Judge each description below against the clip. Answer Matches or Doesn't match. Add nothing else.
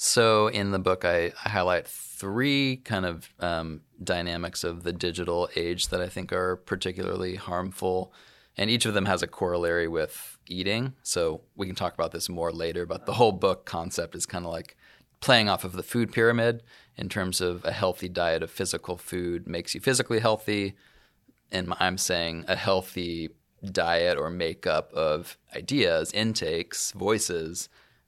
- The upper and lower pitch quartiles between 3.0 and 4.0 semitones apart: Matches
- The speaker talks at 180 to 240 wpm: Doesn't match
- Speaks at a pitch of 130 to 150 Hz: Doesn't match